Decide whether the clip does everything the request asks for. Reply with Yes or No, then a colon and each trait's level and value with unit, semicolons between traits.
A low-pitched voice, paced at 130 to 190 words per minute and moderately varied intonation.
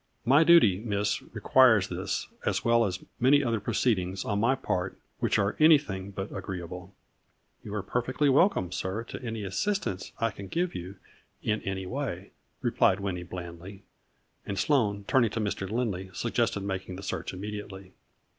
Yes: low, 100 Hz; average, 170 wpm; average, 4.0 semitones